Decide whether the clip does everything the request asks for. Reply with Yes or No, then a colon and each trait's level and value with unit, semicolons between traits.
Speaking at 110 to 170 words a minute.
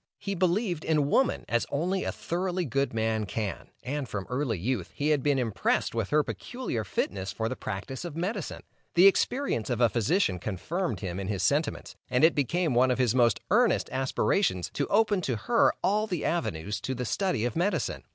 No: average, 195 wpm